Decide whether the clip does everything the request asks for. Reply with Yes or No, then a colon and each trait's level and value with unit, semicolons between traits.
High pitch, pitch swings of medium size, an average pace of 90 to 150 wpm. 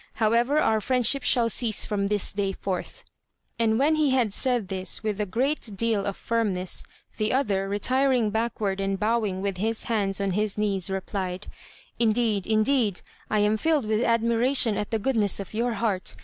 No: high, 215 Hz; average, 3.0 semitones; average, 175 wpm